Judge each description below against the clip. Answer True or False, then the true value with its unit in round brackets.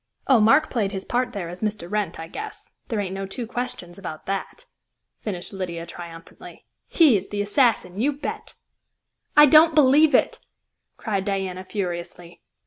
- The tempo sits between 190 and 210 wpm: False (160 wpm)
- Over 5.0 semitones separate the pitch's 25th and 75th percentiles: True (5.5 semitones)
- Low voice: False (200 Hz)